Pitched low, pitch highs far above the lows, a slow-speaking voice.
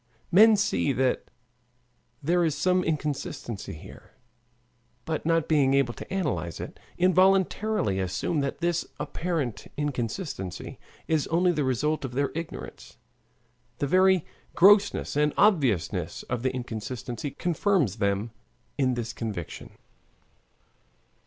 No: medium, 145 Hz; wide, 6.4 semitones; slow, 115 wpm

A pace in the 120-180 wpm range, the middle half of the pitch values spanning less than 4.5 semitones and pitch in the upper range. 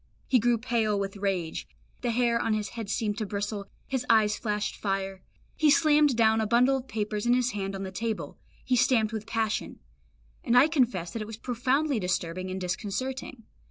No: average, 195 wpm; average, 3.5 semitones; high, 220 Hz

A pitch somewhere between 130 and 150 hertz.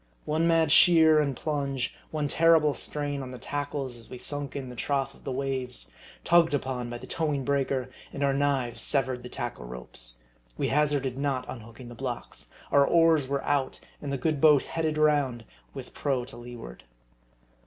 Yes: medium, 140 Hz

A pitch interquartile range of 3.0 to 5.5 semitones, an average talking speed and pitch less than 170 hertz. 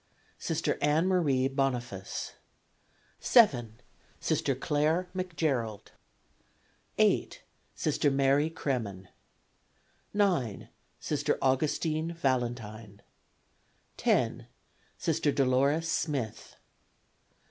No: average, 4.8 semitones; slow, 70 wpm; medium, 140 Hz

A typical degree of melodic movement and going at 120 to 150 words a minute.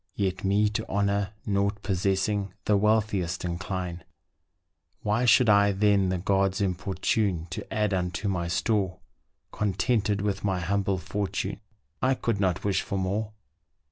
No: narrow, 1.7 semitones; average, 140 wpm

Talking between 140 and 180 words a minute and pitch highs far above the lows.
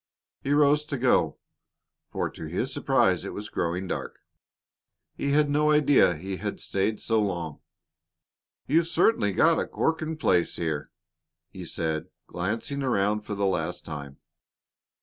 Yes: average, 145 wpm; wide, 8.7 semitones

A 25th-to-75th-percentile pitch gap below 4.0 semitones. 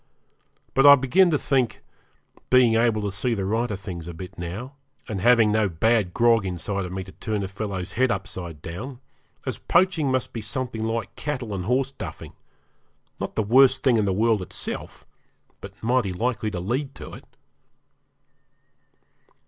No: average, 4.8 semitones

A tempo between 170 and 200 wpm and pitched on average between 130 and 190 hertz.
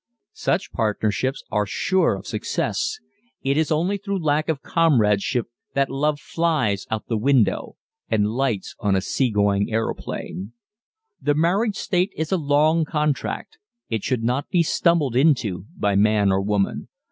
No: average, 155 wpm; low, 135 Hz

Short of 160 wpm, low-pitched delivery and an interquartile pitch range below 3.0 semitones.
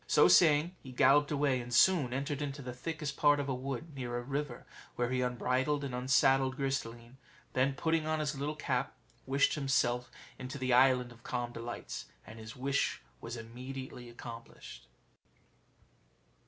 No: average, 170 wpm; low, 130 Hz; narrow, 2.6 semitones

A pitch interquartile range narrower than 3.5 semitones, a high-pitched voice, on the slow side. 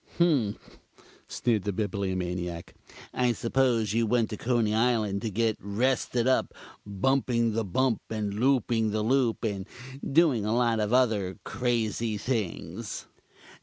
No: average, 3.1 semitones; low, 115 Hz; slow, 130 wpm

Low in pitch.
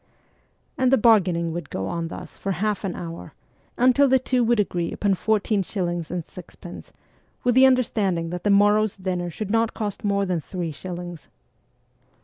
No: high, 195 Hz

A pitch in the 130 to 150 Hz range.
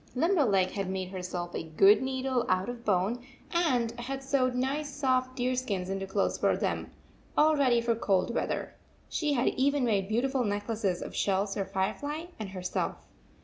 No: high, 235 Hz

